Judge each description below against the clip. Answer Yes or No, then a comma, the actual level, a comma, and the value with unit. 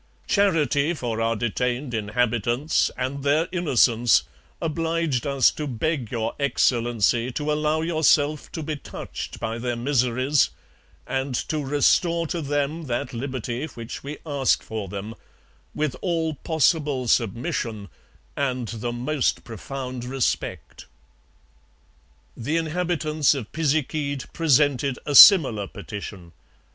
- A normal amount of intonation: Yes, average, 4.4 semitones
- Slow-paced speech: Yes, slow, 115 wpm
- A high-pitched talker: No, low, 135 Hz